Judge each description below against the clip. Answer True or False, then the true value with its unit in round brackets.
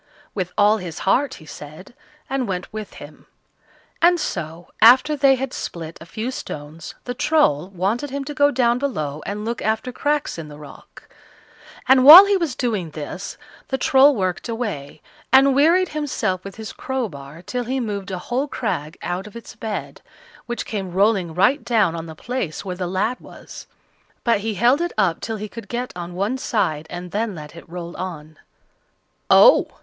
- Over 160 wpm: True (185 wpm)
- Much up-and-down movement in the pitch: True (6.6 semitones)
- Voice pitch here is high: True (210 Hz)